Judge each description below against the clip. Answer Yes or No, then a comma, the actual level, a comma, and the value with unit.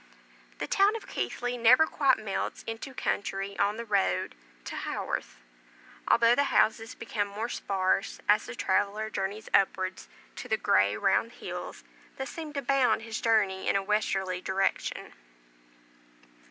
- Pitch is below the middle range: No, high, 215 Hz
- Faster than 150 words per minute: No, average, 145 wpm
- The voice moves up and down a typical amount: Yes, average, 3.7 semitones